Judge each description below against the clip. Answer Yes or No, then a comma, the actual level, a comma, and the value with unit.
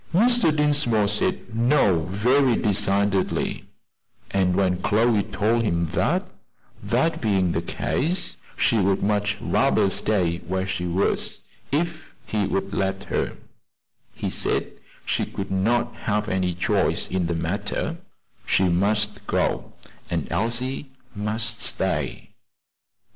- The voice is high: No, low, 105 Hz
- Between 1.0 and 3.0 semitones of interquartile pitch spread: No, average, 3.7 semitones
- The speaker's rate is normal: No, slow, 120 wpm